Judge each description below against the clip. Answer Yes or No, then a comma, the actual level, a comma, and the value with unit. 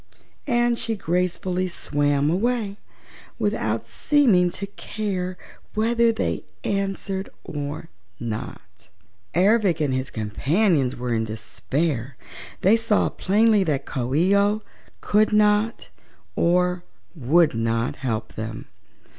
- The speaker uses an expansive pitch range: Yes, wide, 7.3 semitones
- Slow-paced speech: Yes, slow, 110 wpm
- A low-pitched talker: No, medium, 180 Hz